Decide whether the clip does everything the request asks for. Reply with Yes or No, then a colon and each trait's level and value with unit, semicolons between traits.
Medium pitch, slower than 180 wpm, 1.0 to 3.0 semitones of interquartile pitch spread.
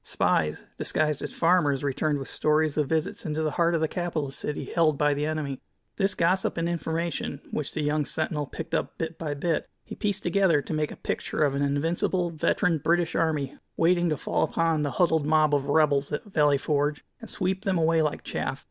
No: medium, 155 Hz; fast, 205 wpm; narrow, 2.4 semitones